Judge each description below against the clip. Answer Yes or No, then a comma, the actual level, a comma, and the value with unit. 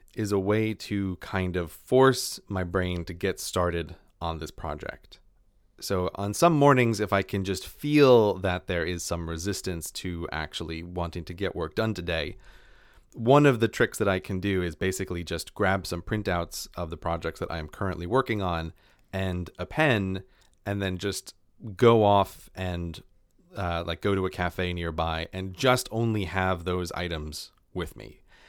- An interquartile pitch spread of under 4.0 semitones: Yes, average, 2.8 semitones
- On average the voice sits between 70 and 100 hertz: Yes, very low, 95 Hz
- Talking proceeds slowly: No, average, 175 wpm